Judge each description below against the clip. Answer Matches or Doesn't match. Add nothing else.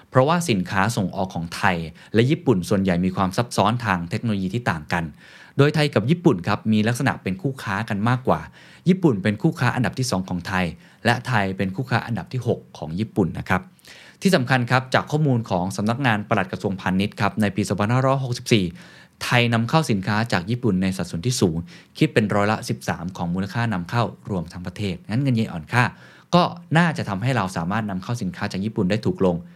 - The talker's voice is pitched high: Doesn't match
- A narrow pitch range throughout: Doesn't match